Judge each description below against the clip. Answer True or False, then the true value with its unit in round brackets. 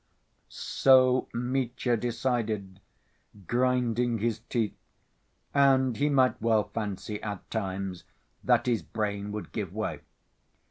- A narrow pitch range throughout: False (3.5 semitones)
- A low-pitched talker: True (115 Hz)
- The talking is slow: True (105 wpm)